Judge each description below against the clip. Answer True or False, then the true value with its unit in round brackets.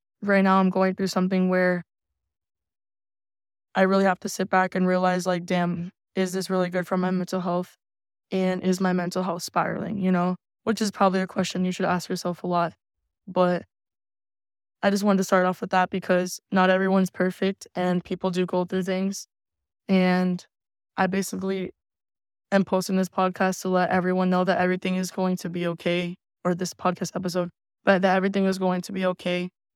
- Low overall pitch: False (185 Hz)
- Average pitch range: False (1.1 semitones)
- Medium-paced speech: True (190 wpm)